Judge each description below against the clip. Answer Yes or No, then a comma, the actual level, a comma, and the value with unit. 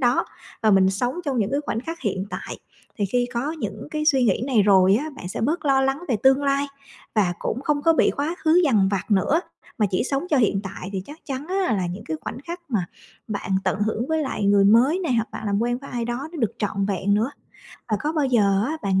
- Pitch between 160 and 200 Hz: No, high, 240 Hz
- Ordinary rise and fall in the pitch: No, wide, 6.1 semitones